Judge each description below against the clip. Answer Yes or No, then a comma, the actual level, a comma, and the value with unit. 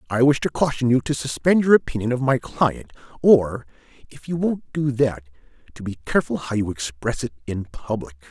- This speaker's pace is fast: No, average, 195 wpm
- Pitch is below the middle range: Yes, low, 125 Hz